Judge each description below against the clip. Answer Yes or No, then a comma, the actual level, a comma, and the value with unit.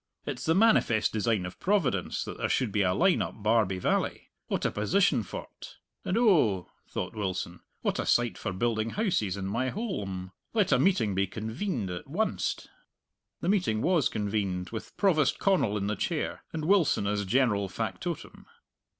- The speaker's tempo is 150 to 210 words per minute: Yes, average, 170 wpm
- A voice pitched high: No, low, 110 Hz